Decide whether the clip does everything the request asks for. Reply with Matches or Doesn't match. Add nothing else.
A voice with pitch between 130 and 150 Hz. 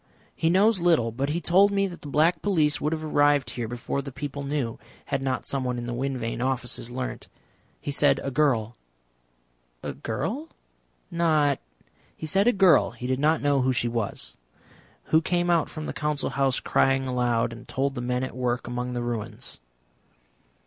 Matches